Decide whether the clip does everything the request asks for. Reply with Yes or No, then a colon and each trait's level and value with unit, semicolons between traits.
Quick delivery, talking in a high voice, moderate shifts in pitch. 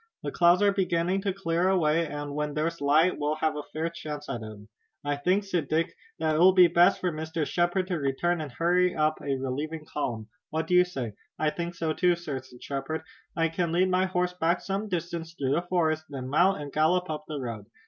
No: fast, 225 wpm; medium, 165 Hz; average, 3.3 semitones